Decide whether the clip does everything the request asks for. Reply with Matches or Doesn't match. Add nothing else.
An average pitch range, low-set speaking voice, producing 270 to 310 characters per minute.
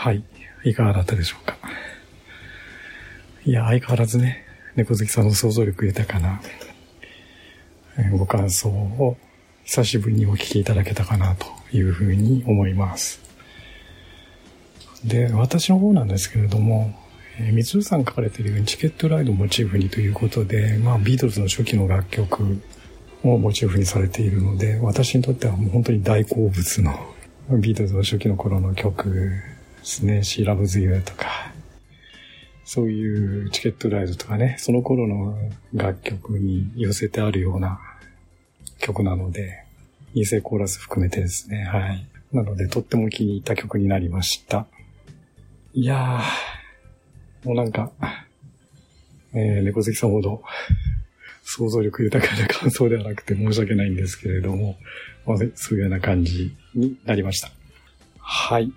Matches